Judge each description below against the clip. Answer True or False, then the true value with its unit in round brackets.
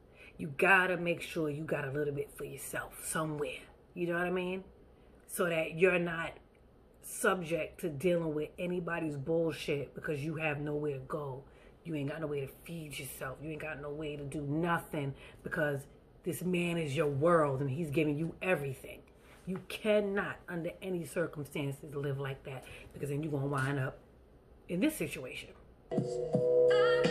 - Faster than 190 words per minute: False (170 wpm)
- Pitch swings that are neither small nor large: True (3.2 semitones)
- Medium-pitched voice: True (155 Hz)